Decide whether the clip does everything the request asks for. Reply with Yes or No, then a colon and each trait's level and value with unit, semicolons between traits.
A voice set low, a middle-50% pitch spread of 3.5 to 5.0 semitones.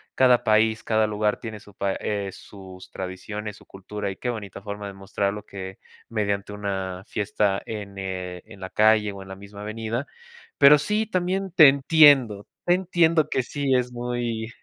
Yes: low, 105 Hz; average, 3.8 semitones